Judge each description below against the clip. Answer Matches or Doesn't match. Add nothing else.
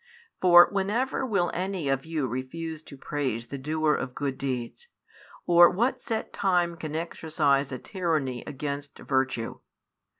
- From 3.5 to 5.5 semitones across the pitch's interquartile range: Matches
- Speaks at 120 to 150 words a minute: Matches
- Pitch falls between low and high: Matches